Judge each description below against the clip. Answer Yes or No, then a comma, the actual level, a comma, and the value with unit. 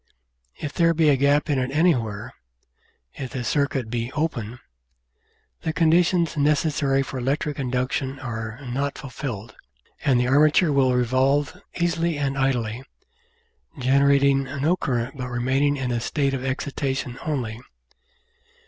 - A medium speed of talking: No, slow, 130 wpm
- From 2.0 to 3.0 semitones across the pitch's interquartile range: Yes, average, 2.7 semitones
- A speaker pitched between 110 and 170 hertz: Yes, low, 135 Hz